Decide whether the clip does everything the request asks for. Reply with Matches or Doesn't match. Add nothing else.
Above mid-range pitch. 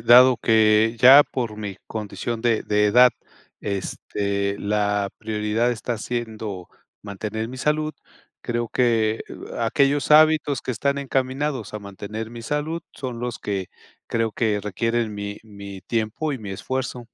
Doesn't match